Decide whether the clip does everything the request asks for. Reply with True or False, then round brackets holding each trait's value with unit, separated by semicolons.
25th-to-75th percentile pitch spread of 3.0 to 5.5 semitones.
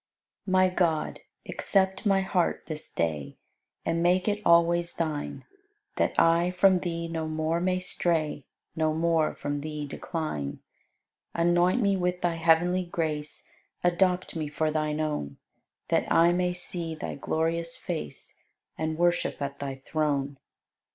False (2.5 semitones)